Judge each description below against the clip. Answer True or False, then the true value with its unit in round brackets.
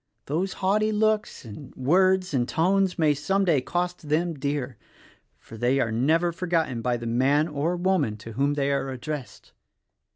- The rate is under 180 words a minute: True (165 wpm)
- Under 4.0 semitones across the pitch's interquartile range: False (5.4 semitones)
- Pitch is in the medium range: True (150 Hz)